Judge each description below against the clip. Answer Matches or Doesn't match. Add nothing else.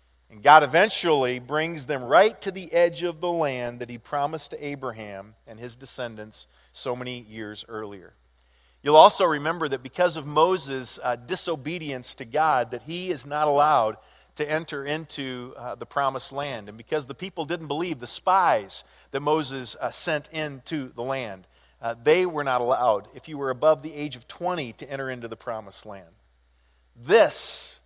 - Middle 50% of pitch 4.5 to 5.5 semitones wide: Matches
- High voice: Doesn't match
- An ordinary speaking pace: Matches